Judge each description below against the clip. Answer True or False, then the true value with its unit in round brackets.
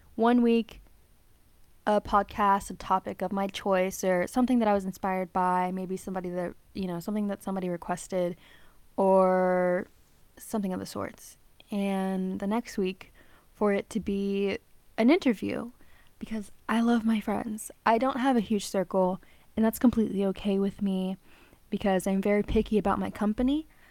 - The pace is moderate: True (160 wpm)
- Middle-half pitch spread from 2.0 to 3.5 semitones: True (2.8 semitones)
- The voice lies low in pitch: False (200 Hz)